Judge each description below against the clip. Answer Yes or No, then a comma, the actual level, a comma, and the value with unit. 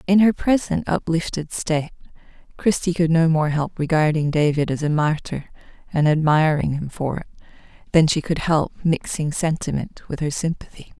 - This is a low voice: No, medium, 160 Hz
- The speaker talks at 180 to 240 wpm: No, average, 160 wpm